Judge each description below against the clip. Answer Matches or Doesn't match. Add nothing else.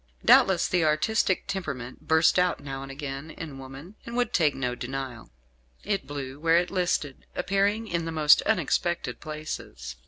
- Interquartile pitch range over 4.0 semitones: Matches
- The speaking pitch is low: Doesn't match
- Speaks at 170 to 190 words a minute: Doesn't match